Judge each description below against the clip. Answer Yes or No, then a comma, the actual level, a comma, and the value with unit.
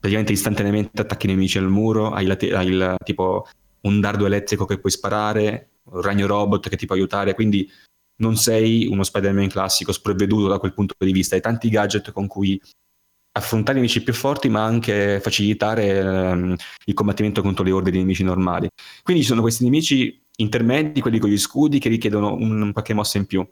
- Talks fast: Yes, fast, 195 wpm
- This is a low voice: Yes, low, 100 Hz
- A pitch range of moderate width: No, narrow, 2.1 semitones